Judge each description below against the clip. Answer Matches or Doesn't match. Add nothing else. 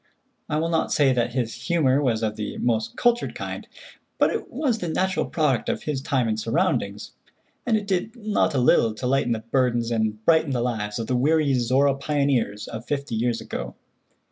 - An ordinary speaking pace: Matches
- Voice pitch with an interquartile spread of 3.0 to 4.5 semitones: Doesn't match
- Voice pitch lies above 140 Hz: Doesn't match